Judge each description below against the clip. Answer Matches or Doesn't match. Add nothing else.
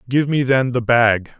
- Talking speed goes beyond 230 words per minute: Doesn't match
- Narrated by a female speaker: Doesn't match